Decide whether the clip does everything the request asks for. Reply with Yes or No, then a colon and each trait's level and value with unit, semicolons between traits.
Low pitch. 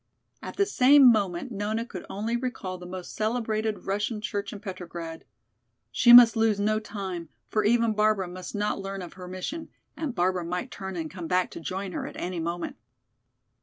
No: high, 200 Hz